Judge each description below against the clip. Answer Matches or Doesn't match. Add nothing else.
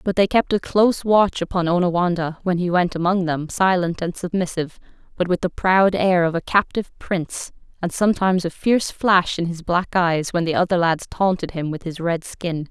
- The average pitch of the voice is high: Doesn't match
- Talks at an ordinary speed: Doesn't match